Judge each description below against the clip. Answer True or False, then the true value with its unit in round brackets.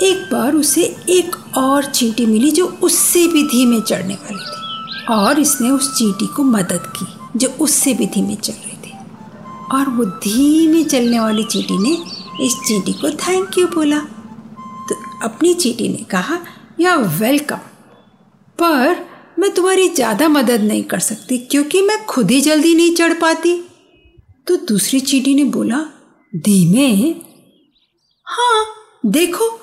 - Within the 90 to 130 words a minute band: False (145 wpm)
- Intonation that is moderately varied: False (7.1 semitones)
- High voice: True (270 Hz)